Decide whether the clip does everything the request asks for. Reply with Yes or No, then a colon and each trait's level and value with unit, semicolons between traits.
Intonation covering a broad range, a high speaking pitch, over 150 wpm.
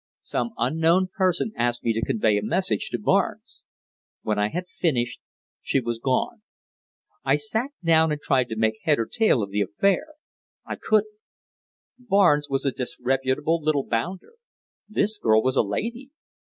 No: wide, 8.5 semitones; medium, 145 Hz; average, 160 wpm